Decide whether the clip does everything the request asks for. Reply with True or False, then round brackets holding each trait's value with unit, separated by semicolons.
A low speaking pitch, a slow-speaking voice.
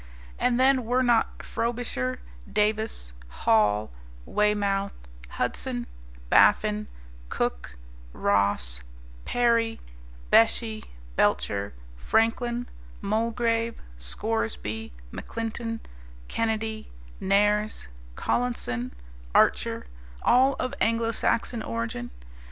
False (215 Hz; 75 wpm)